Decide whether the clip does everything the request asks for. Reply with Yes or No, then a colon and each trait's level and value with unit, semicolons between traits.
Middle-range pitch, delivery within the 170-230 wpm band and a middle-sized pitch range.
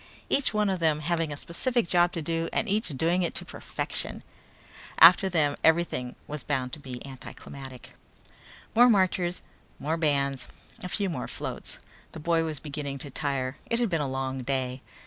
Yes: medium, 155 Hz; average, 175 wpm; average, 4.2 semitones